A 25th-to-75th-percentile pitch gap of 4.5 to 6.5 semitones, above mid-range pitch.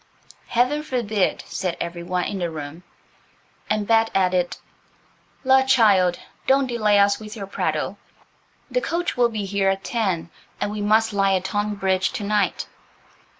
No: average, 3.3 semitones; high, 205 Hz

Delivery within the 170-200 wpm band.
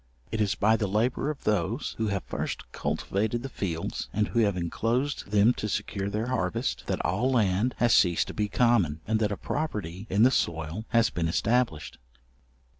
Yes: average, 190 wpm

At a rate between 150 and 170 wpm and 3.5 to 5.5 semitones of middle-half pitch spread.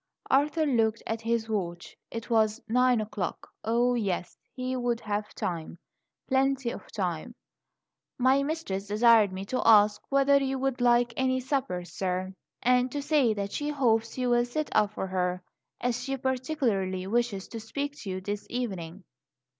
Yes: average, 160 wpm; average, 4.4 semitones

